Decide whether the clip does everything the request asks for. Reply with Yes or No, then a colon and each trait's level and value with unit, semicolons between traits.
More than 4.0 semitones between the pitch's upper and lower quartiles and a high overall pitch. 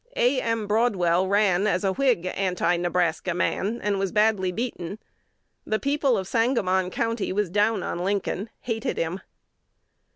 No: average, 3.7 semitones; high, 200 Hz